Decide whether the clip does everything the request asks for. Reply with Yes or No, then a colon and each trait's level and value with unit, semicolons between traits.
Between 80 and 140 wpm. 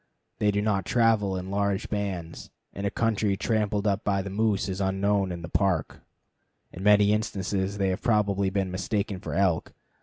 No: average, 175 wpm